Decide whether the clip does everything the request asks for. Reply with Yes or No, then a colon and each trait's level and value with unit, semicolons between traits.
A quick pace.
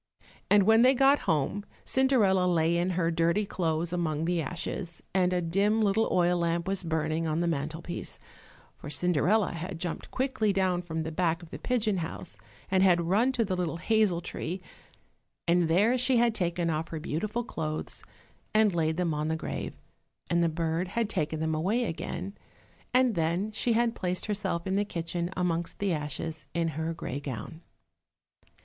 No: average, 180 wpm